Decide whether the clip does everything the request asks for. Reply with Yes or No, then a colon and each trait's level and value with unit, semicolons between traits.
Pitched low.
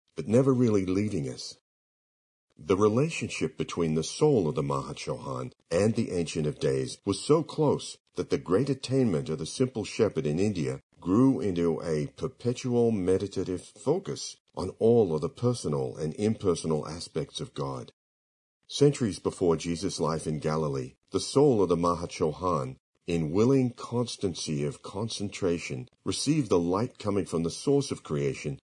Yes: low, 100 Hz